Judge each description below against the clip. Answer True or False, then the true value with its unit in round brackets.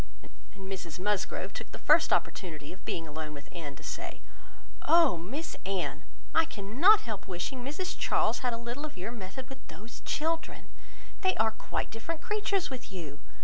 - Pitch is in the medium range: False (220 Hz)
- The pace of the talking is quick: False (175 wpm)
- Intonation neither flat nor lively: False (8.2 semitones)